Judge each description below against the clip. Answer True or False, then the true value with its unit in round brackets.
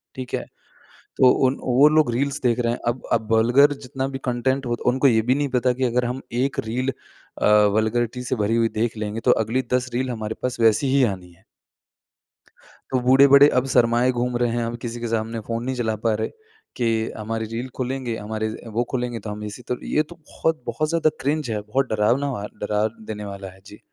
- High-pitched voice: False (120 Hz)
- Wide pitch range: False (2.8 semitones)